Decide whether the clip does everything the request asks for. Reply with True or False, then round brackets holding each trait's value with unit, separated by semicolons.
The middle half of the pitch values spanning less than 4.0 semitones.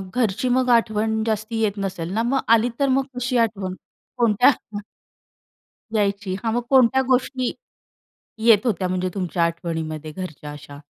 False (4.6 semitones)